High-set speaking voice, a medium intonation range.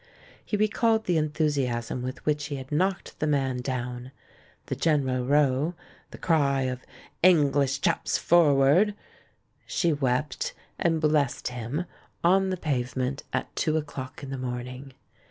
No: medium, 140 Hz; average, 3.6 semitones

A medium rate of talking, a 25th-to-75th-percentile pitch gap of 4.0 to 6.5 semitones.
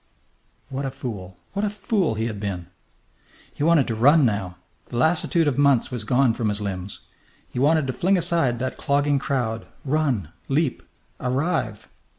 Yes: average, 165 wpm; wide, 5.6 semitones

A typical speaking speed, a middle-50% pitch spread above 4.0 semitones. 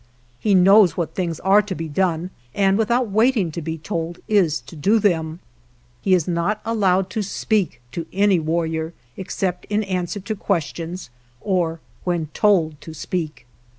No: average, 165 wpm; average, 3.7 semitones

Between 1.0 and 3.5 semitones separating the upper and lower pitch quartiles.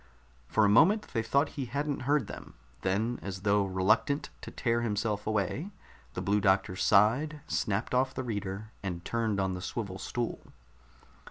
No: average, 4.5 semitones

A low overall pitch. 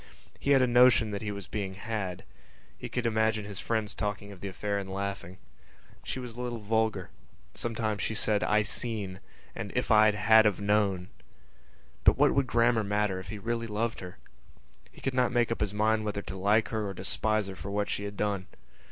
Yes: low, 105 Hz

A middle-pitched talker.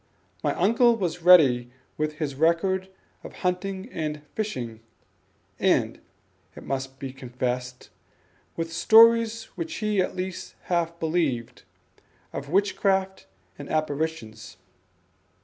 Yes: medium, 165 Hz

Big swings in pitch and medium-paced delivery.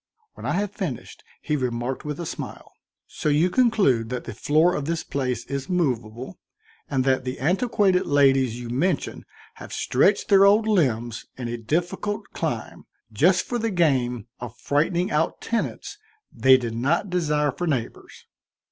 Yes: wide, 6.2 semitones; average, 160 wpm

